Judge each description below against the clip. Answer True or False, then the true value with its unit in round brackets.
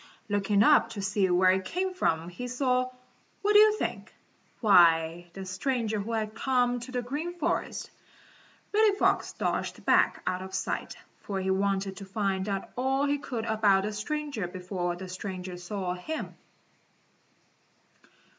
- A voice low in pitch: False (205 Hz)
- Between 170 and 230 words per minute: False (155 wpm)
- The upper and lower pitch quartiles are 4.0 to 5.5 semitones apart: True (5.2 semitones)